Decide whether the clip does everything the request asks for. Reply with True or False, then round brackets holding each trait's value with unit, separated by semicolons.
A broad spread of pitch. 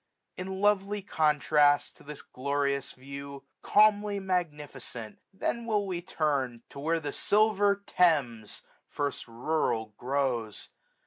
True (5.7 semitones)